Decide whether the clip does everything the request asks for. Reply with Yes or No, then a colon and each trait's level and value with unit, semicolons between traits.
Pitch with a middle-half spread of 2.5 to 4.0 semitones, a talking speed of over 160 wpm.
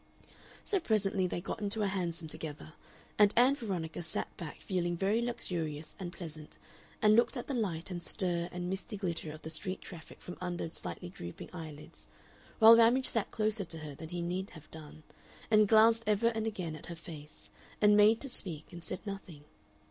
No: average, 4.8 semitones; average, 190 wpm